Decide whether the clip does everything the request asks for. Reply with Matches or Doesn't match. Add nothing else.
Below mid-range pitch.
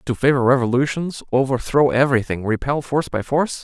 Matches